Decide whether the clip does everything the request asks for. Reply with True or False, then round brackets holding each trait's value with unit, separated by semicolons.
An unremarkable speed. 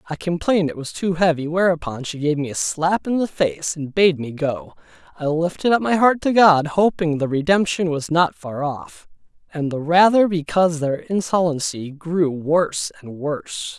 True (185 wpm)